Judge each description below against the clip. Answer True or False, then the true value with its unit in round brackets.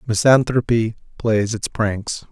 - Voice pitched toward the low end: True (110 Hz)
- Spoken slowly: True (105 wpm)